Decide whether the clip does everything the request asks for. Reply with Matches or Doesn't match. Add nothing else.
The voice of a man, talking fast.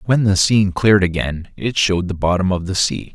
Matches